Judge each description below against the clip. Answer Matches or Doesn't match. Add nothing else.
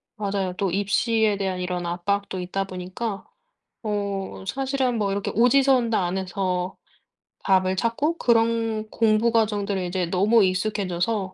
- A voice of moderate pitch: Doesn't match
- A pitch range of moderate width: Matches